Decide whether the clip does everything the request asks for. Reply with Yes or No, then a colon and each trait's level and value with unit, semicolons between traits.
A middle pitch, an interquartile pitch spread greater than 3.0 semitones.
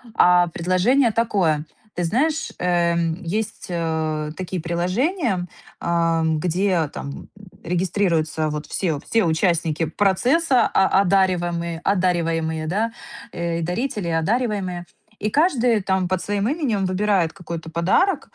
Yes: medium, 180 Hz; average, 3.8 semitones